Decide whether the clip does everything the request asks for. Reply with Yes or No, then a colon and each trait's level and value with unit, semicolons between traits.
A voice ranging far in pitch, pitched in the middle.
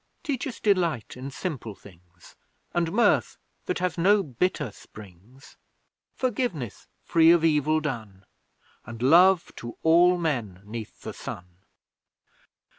Yes: wide, 8.4 semitones; medium, 150 Hz